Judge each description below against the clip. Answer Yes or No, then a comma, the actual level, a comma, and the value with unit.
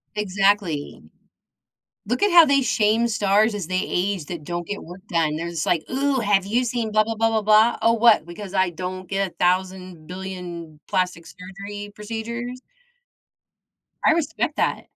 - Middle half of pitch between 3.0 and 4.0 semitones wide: Yes, average, 3.7 semitones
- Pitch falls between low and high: No, high, 200 Hz